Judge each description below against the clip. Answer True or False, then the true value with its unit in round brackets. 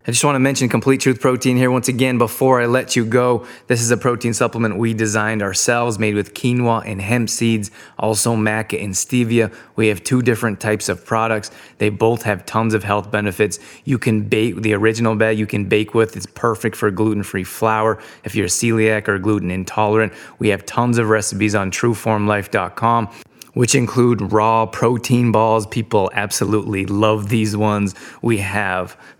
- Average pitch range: False (2.0 semitones)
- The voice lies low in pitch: True (110 Hz)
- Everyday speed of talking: True (180 wpm)